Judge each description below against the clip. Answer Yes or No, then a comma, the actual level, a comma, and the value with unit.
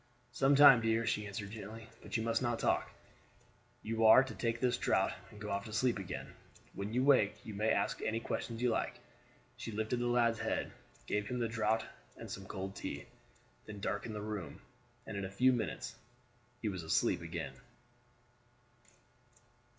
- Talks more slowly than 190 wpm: Yes, average, 180 wpm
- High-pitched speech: No, low, 110 Hz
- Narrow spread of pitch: Yes, narrow, 2.3 semitones